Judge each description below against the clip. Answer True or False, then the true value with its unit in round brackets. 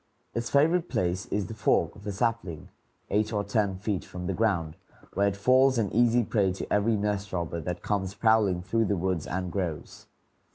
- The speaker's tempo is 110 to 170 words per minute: False (195 wpm)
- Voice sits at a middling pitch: False (100 Hz)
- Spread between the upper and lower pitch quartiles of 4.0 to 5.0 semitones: False (3.3 semitones)